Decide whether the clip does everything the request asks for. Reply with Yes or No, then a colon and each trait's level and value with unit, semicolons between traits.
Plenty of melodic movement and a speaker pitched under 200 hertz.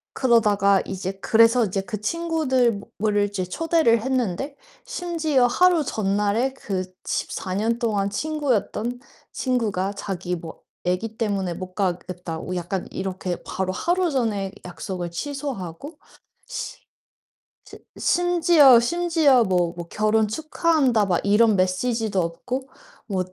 No: wide, 6.1 semitones; high, 215 Hz